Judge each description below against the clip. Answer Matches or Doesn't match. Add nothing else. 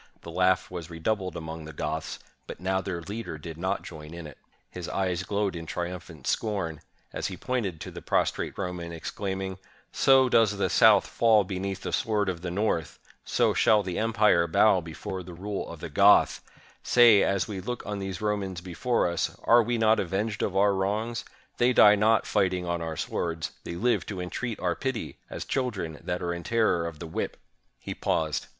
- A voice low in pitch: Matches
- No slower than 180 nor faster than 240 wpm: Matches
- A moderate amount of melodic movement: Matches